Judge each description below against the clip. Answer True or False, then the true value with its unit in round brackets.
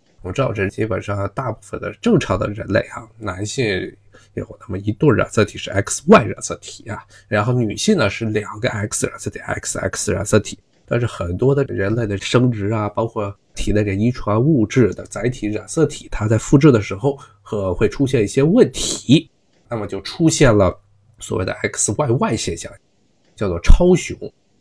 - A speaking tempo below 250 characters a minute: False (265 characters per minute)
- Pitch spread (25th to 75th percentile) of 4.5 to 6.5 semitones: False (3.4 semitones)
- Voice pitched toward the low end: True (110 Hz)